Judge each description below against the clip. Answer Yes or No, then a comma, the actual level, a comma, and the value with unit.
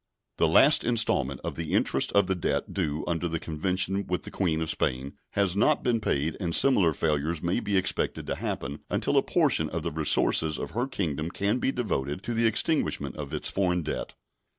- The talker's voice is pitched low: Yes, very low, 85 Hz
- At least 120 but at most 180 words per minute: No, average, 200 wpm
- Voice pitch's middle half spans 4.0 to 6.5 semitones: Yes, average, 4.7 semitones